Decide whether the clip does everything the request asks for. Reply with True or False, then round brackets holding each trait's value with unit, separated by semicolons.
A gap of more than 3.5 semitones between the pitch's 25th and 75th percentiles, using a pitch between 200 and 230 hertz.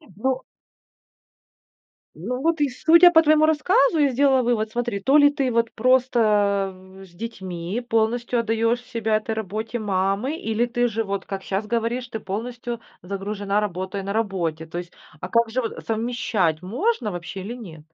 True (4.0 semitones; 225 Hz)